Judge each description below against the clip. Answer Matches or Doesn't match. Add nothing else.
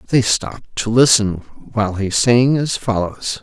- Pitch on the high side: Doesn't match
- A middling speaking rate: Matches